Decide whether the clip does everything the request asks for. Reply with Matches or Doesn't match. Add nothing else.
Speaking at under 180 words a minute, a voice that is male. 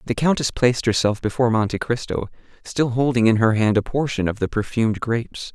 Doesn't match